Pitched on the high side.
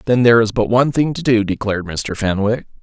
No: low, 110 Hz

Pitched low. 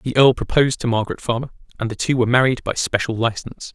Yes: low, 120 Hz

